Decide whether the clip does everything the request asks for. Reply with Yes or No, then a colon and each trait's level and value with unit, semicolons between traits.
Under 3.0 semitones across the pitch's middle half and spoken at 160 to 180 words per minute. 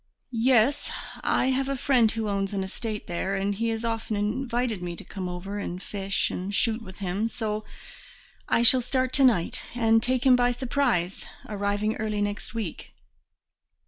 No: average, 3.5 semitones; average, 175 wpm